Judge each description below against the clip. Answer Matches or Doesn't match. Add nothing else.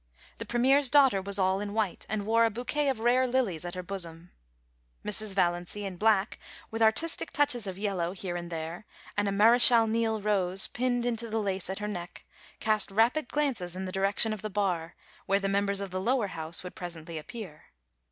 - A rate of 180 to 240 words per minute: Matches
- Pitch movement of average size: Matches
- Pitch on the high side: Matches